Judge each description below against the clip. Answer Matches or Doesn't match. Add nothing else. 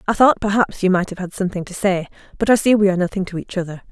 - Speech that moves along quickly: Matches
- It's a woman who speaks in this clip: Matches